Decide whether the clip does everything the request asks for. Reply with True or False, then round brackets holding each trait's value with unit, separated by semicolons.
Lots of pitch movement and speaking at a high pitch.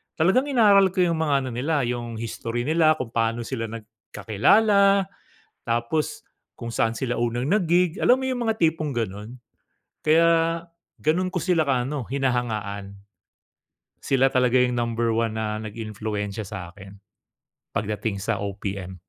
False (6.8 semitones; 120 Hz)